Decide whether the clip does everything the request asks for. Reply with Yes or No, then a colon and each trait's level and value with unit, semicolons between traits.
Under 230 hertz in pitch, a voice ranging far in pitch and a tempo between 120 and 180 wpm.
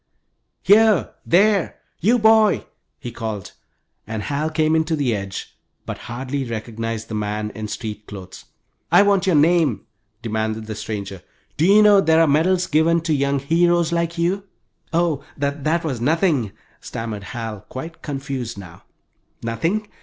Yes: medium, 140 Hz; wide, 7.3 semitones; average, 150 wpm